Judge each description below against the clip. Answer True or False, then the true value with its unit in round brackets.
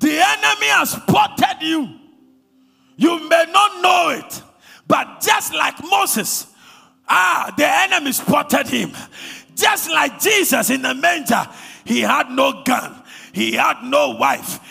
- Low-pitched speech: False (325 Hz)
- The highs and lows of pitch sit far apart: True (6.0 semitones)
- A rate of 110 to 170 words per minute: True (135 wpm)